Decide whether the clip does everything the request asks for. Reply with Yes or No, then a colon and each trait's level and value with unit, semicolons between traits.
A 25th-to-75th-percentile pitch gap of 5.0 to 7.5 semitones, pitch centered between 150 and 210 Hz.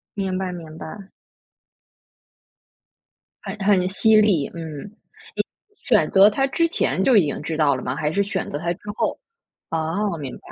No: average, 4.4 semitones; medium, 185 Hz